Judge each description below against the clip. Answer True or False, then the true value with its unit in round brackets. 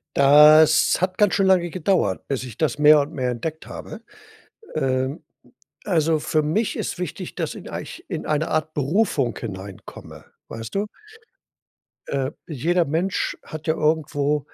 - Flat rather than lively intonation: False (3.8 semitones)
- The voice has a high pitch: False (155 Hz)